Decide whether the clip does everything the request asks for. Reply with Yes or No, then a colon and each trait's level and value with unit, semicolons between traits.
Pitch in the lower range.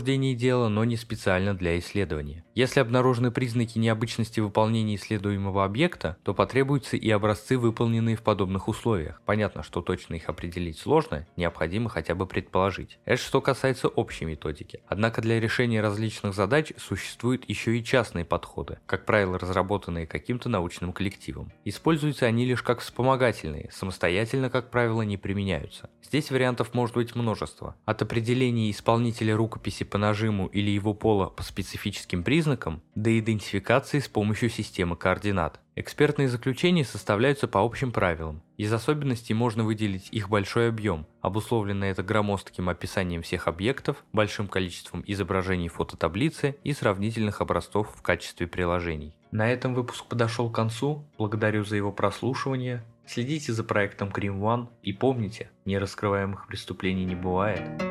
Yes: low, 110 Hz